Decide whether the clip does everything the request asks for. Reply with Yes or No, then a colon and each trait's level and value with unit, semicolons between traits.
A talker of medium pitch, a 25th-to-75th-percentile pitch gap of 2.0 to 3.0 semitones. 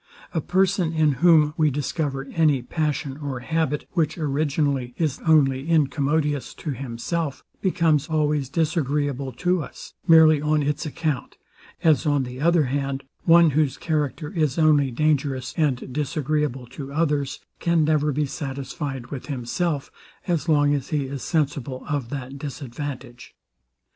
Yes: medium, 145 Hz; narrow, 2.6 semitones